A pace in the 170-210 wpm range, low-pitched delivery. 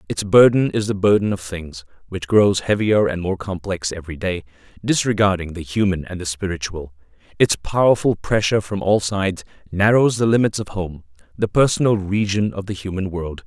Yes: average, 175 wpm; very low, 95 Hz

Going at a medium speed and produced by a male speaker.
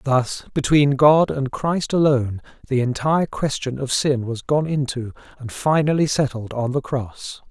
Yes: average, 160 wpm; male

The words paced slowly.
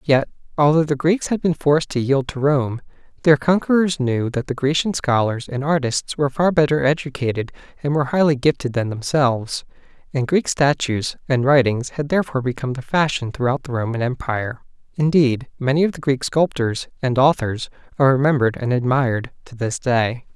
No: average, 175 wpm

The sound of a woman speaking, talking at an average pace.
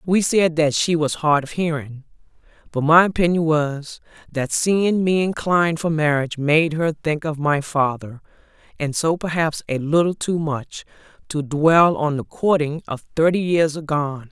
Yes: female; average, 170 wpm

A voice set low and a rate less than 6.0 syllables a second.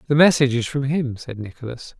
No: low, 130 Hz; 6.1 syllables/s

